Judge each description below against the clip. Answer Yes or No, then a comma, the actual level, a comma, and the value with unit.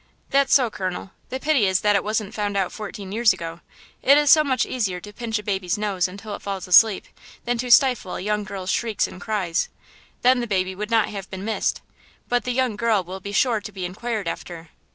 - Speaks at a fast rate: Yes, fast, 215 wpm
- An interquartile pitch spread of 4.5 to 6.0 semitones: No, average, 3.9 semitones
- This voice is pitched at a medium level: No, high, 210 Hz